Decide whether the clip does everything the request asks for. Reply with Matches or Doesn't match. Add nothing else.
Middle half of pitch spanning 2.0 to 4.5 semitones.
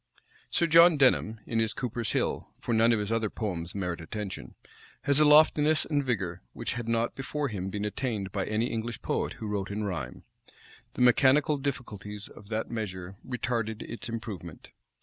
Matches